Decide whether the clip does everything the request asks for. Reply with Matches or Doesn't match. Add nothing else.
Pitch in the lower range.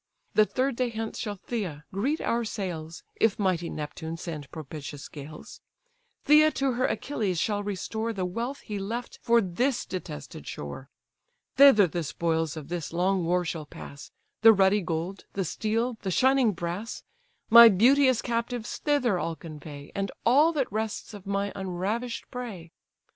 Doesn't match